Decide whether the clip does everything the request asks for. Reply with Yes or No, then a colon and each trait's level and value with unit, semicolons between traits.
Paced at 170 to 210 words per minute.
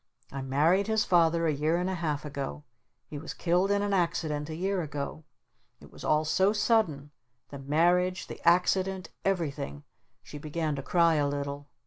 Yes: average, 180 wpm